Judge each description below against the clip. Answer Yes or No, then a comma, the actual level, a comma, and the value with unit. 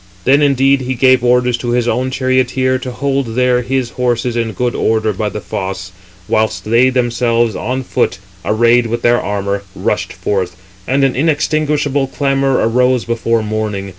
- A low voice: Yes, low, 125 Hz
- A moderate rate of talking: Yes, average, 165 wpm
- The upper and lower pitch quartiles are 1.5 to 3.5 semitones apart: Yes, narrow, 2.5 semitones